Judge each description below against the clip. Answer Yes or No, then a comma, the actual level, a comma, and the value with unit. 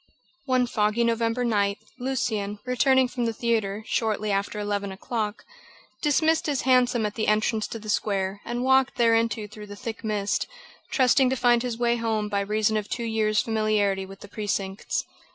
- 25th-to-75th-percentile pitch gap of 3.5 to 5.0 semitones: No, narrow, 2.6 semitones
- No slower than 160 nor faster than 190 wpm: Yes, average, 170 wpm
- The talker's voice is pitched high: Yes, high, 220 Hz